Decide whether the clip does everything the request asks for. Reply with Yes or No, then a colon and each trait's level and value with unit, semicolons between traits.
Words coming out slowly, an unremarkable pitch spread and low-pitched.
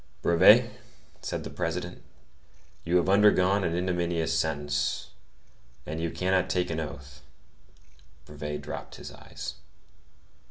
Yes: slow, 115 wpm; average, 3.5 semitones; very low, 80 Hz